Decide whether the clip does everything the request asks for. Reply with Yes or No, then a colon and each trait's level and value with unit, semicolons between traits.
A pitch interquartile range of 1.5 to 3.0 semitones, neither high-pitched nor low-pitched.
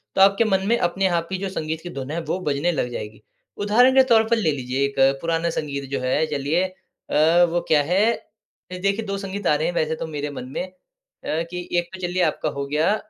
No: average, 4.4 semitones; medium, 170 Hz